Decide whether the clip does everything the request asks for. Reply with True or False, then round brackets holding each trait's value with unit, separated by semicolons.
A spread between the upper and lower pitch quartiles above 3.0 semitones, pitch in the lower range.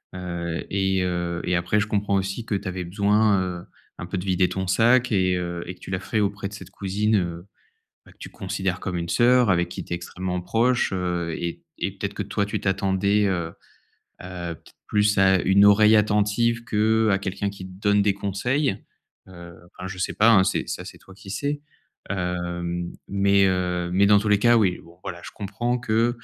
False (2.7 semitones; 95 Hz)